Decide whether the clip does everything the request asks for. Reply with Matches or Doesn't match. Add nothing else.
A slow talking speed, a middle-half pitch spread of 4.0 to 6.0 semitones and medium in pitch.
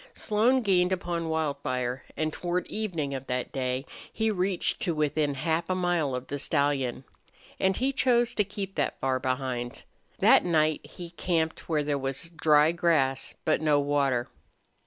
Doesn't match